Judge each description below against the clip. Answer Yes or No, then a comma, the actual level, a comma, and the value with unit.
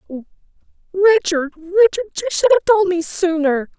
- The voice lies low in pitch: No, very high, 365 Hz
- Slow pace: No, average, 145 wpm